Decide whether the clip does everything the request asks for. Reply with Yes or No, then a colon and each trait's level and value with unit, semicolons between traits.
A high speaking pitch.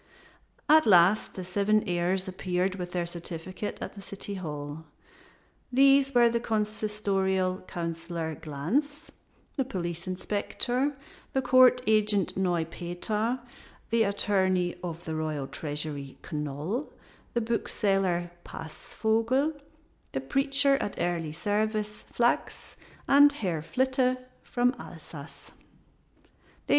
Yes: high, 195 Hz